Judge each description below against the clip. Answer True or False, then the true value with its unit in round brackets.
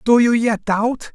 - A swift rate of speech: True (210 wpm)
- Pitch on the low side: False (230 Hz)